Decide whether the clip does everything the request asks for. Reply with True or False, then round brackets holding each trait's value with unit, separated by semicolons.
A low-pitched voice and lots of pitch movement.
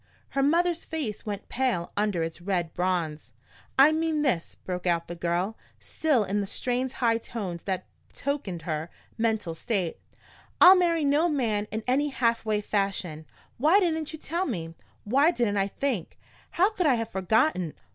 False (220 Hz; 8.0 semitones)